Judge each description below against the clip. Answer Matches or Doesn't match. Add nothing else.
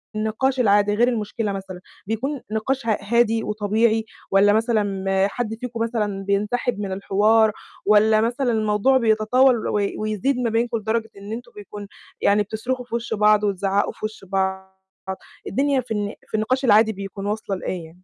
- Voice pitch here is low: Doesn't match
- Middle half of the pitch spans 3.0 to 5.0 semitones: Doesn't match